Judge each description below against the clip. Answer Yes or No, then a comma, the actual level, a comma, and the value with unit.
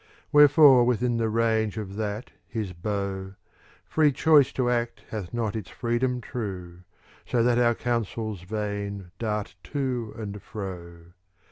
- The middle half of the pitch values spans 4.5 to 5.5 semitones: No, average, 3.4 semitones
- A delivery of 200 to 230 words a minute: No, average, 140 wpm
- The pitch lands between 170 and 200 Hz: No, low, 110 Hz